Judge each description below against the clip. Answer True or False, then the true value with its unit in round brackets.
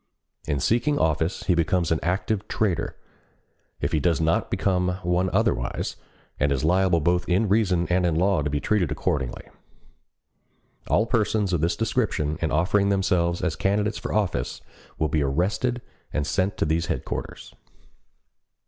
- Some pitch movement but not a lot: True (3.9 semitones)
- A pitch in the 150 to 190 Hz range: False (90 Hz)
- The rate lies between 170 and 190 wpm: False (155 wpm)